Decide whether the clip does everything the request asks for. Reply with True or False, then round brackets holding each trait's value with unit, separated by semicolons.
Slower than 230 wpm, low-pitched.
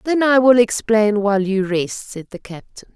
False (205 wpm; 215 Hz)